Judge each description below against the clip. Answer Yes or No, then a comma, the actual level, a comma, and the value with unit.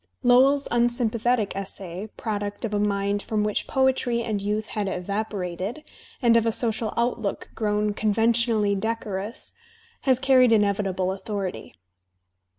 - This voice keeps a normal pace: No, slow, 130 wpm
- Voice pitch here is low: No, high, 215 Hz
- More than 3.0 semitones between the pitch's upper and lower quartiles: No, average, 2.7 semitones